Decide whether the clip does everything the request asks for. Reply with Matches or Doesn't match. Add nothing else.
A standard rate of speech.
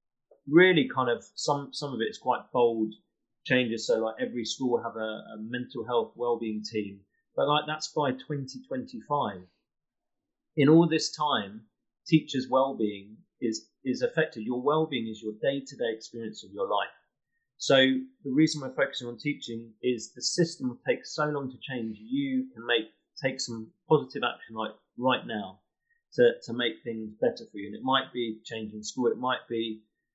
Matches